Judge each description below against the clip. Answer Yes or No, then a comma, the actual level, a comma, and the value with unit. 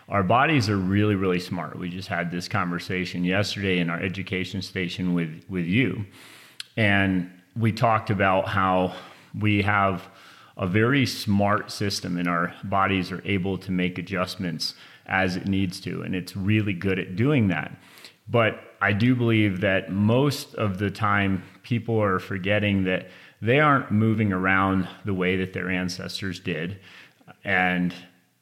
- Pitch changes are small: Yes, narrow, 2.3 semitones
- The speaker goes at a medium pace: Yes, average, 155 wpm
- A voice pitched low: Yes, very low, 95 Hz